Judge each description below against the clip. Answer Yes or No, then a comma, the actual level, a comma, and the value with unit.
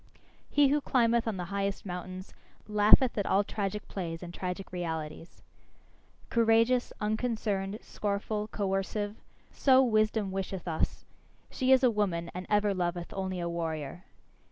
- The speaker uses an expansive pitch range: No, average, 3.4 semitones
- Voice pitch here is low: No, high, 200 Hz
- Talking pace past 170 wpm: No, slow, 135 wpm